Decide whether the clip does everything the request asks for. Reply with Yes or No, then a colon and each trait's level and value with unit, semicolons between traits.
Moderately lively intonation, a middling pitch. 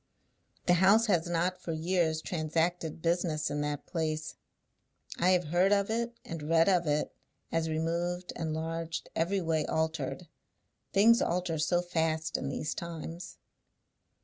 No: narrow, 1.9 semitones; medium, 165 Hz